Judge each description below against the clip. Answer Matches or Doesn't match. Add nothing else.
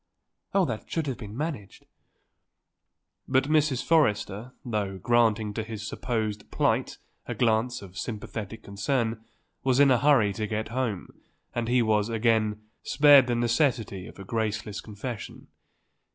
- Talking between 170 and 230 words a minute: Doesn't match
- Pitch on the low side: Matches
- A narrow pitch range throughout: Doesn't match